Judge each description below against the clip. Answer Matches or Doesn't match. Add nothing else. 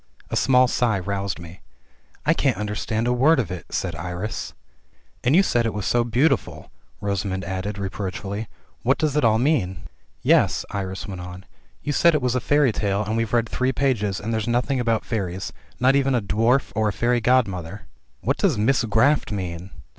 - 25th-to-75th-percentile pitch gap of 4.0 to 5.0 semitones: Matches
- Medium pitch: Doesn't match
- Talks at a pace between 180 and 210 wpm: Matches